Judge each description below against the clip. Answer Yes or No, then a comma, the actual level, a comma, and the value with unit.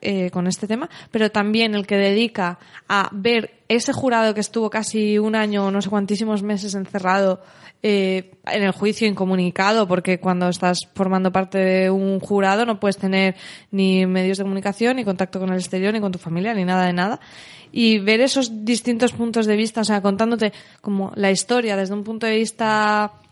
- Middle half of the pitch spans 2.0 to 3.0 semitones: Yes, narrow, 2.5 semitones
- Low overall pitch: No, high, 200 Hz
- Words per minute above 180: Yes, fast, 190 wpm